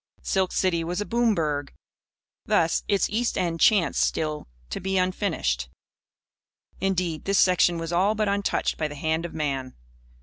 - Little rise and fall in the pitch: No, average, 3.7 semitones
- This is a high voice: No, medium, 175 Hz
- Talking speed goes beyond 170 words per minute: No, average, 160 wpm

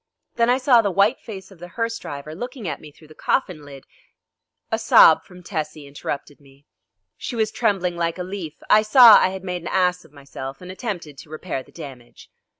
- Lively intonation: Yes, wide, 5.7 semitones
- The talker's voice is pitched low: No, medium, 180 Hz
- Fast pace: Yes, fast, 215 wpm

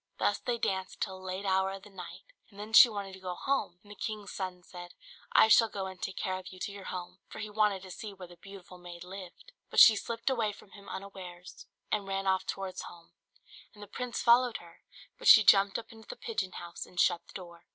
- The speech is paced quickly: Yes, fast, 245 wpm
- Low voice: No, high, 195 Hz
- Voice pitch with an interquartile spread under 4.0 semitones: Yes, narrow, 2.4 semitones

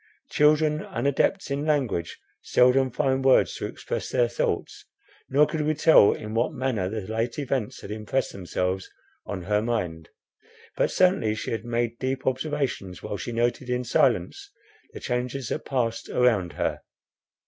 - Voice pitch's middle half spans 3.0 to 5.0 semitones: Yes, average, 4.1 semitones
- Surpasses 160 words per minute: No, average, 155 wpm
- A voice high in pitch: No, low, 125 Hz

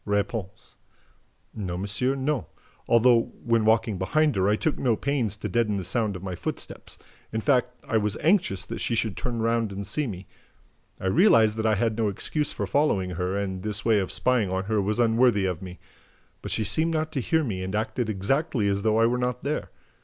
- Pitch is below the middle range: Yes, low, 110 Hz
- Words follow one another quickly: Yes, fast, 215 wpm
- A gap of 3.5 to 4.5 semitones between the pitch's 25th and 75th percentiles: Yes, average, 4.0 semitones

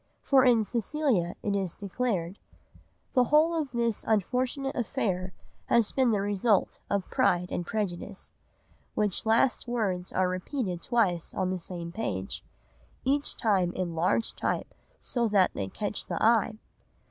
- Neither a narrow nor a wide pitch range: Yes, average, 4.8 semitones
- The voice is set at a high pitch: Yes, high, 210 Hz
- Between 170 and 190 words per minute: No, average, 145 wpm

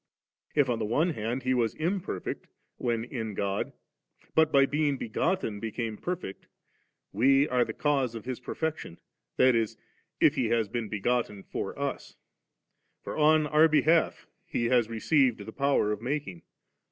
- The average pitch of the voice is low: Yes, low, 125 Hz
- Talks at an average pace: Yes, average, 160 wpm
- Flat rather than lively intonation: No, average, 5.0 semitones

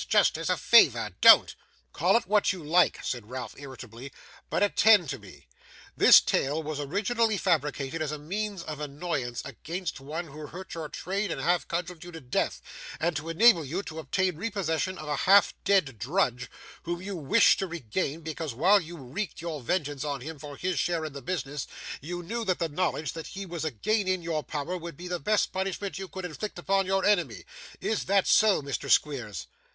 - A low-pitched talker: No, medium, 165 Hz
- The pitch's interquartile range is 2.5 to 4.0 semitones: No, average, 4.4 semitones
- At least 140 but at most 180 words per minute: No, average, 200 wpm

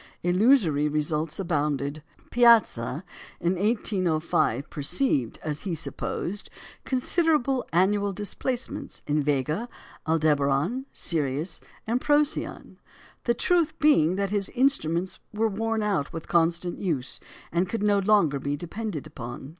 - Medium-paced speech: No, slow, 115 wpm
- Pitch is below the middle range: No, medium, 180 Hz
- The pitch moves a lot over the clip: Yes, wide, 6.6 semitones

